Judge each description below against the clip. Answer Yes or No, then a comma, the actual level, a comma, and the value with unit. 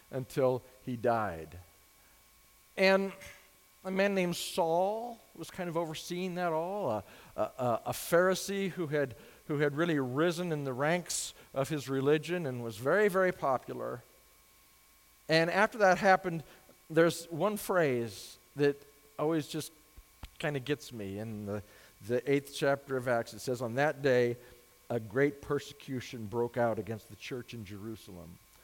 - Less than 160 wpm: Yes, average, 150 wpm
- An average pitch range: No, wide, 6.3 semitones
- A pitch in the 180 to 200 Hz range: No, medium, 140 Hz